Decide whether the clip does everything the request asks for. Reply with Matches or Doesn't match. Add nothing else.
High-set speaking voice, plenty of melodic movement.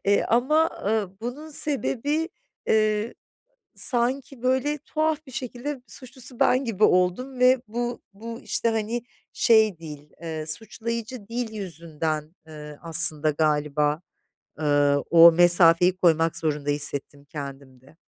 Matches